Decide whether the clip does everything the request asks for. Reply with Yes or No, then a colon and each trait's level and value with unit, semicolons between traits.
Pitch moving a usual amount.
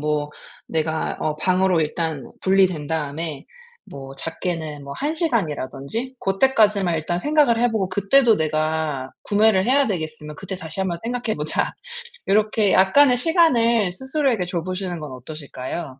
No: wide, 6.4 semitones